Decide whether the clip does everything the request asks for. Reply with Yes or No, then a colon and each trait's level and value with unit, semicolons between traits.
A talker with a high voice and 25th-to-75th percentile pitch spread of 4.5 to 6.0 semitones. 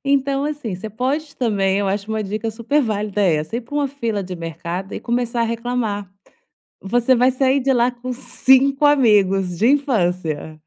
Yes: high, 230 Hz; average, 5.1 semitones